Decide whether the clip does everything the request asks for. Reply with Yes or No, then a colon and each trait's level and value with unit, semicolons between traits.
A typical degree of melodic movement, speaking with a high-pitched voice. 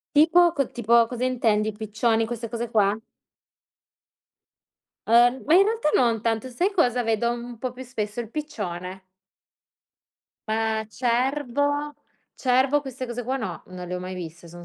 Yes: average, 3.3 semitones; high, 235 Hz